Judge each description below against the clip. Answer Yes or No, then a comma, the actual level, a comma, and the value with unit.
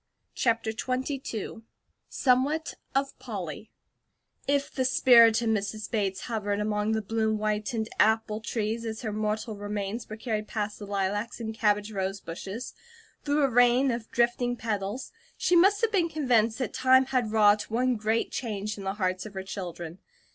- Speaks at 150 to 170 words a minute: Yes, average, 160 wpm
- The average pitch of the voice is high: Yes, high, 220 Hz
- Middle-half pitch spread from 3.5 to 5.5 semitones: No, average, 2.9 semitones